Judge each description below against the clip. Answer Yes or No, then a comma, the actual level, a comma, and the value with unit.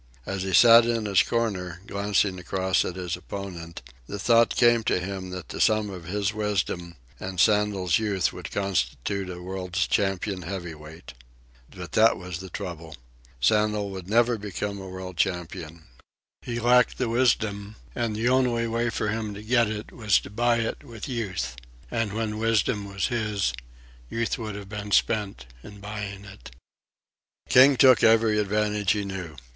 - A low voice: Yes, low, 100 Hz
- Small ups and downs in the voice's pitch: No, average, 3.3 semitones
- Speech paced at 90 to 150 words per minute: No, average, 165 wpm